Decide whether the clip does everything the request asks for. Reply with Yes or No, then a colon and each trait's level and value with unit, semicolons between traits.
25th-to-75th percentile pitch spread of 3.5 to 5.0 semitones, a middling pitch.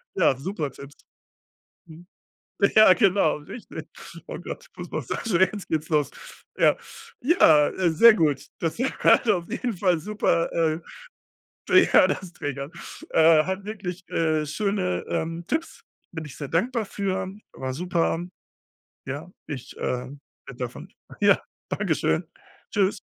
Yes: average, 4.4 semitones; medium, 170 Hz